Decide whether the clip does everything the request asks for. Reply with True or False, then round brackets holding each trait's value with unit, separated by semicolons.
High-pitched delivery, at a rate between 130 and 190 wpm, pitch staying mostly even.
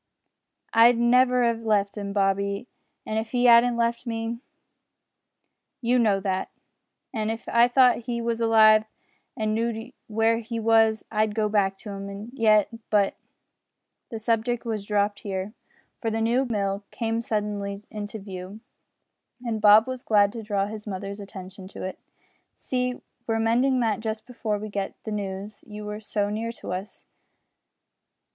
True (220 Hz; 155 wpm; 2.3 semitones)